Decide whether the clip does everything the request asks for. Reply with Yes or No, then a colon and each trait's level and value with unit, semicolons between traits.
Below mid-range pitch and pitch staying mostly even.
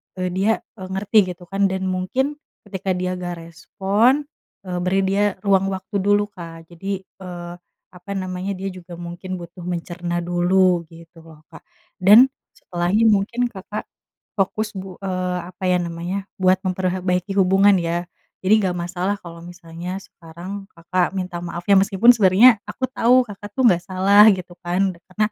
No: medium, 185 Hz; narrow, 2.1 semitones